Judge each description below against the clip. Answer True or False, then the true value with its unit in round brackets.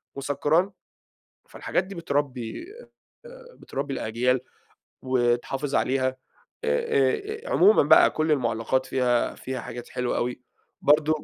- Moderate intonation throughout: True (3.5 semitones)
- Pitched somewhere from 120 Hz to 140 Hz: True (135 Hz)